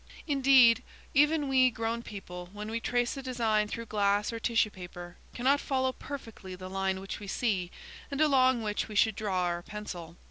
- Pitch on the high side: Yes, high, 220 Hz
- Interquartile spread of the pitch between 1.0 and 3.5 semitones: No, average, 5.0 semitones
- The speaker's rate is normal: Yes, average, 180 wpm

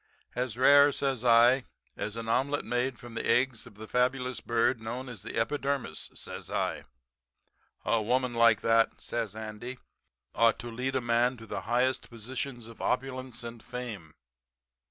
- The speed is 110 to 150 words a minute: No, average, 160 wpm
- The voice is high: No, low, 120 Hz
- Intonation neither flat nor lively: No, narrow, 2.1 semitones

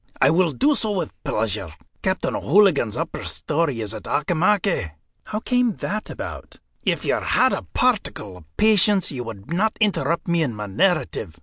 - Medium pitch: Yes, medium, 165 Hz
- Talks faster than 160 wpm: Yes, average, 170 wpm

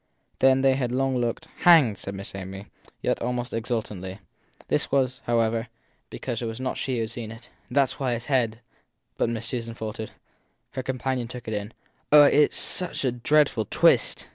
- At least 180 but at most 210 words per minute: Yes, average, 185 wpm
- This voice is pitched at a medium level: No, low, 120 Hz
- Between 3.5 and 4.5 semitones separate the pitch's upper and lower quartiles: No, average, 2.8 semitones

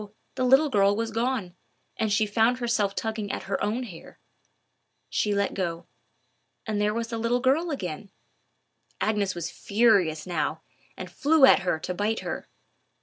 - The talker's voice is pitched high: Yes, high, 215 Hz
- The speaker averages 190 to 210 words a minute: No, average, 160 wpm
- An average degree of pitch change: Yes, average, 3.3 semitones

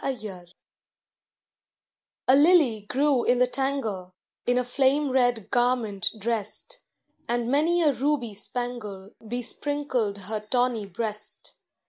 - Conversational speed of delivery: No, slow, 110 wpm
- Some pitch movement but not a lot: Yes, average, 4.0 semitones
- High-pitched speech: Yes, high, 245 Hz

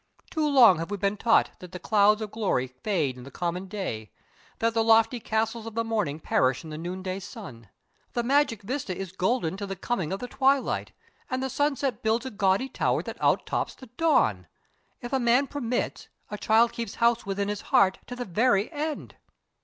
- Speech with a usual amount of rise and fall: Yes, average, 4.7 semitones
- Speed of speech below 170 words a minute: No, fast, 205 wpm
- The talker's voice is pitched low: No, high, 215 Hz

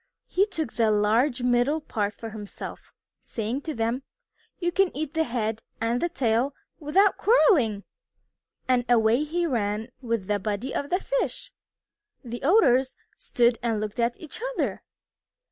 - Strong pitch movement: Yes, wide, 5.8 semitones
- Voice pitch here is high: Yes, high, 245 Hz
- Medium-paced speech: Yes, average, 150 wpm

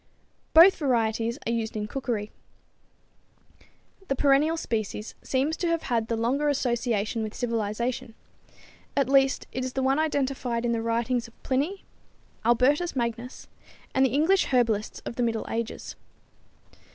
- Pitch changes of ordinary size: Yes, average, 3.1 semitones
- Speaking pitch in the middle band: No, high, 245 Hz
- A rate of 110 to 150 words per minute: Yes, average, 140 wpm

